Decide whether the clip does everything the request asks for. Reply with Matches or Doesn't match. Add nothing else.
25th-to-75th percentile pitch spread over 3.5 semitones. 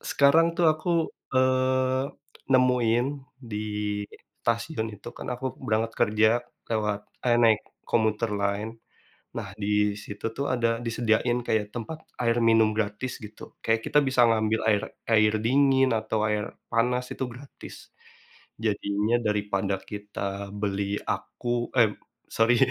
Doesn't match